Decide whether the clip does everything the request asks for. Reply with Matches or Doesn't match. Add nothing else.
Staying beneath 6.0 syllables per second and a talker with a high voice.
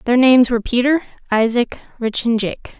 Matches